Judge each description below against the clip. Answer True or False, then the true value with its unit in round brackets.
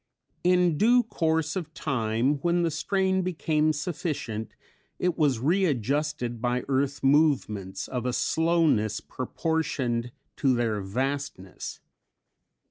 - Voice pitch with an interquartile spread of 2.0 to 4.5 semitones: False (5.1 semitones)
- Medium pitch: True (145 Hz)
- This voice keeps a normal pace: False (110 wpm)